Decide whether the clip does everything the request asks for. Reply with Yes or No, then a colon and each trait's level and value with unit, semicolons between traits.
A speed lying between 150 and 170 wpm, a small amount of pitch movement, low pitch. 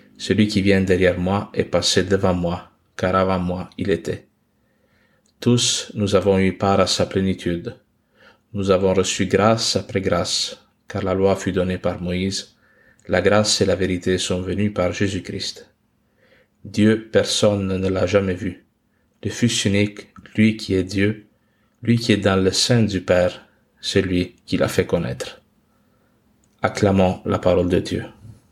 Yes: average, 160 wpm; narrow, 2.3 semitones; low, 100 Hz